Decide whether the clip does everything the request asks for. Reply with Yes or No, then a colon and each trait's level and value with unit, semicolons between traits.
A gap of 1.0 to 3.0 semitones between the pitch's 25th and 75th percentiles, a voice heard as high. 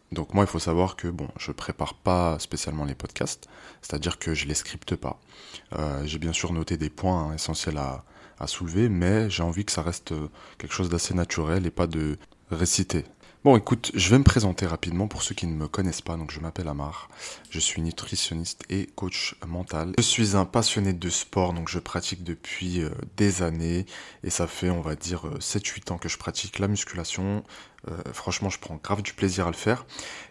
No: average, 2.7 semitones; very low, 85 Hz